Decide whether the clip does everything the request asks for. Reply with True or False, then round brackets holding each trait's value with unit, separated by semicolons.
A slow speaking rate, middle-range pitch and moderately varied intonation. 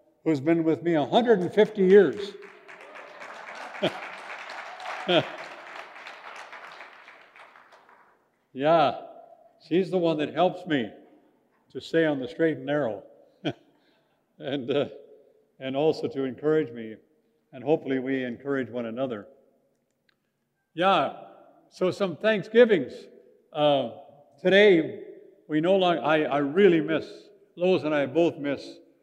False (105 wpm; 165 Hz; 6.6 semitones)